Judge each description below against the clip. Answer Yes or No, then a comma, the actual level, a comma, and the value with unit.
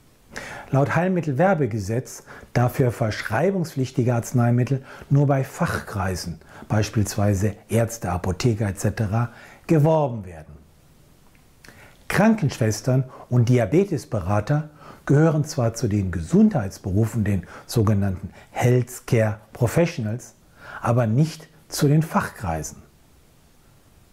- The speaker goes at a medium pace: No, slow, 80 wpm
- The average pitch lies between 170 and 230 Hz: No, low, 120 Hz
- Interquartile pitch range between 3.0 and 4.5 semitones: No, wide, 5.6 semitones